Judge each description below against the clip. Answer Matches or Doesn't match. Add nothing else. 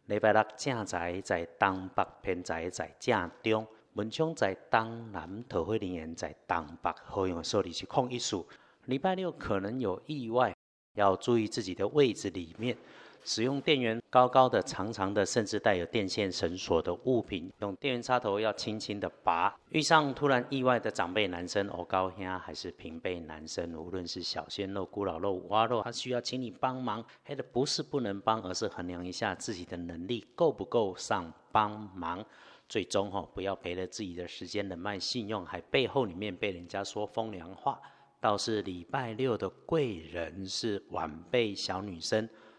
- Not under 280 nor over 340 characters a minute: Doesn't match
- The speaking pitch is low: Matches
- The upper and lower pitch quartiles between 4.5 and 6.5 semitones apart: Matches